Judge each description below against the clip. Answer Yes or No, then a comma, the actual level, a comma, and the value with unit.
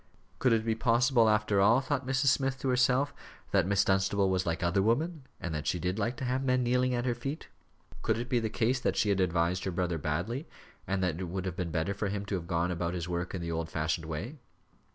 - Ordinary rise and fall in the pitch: No, wide, 5.9 semitones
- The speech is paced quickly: Yes, fast, 250 wpm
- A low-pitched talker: Yes, low, 100 Hz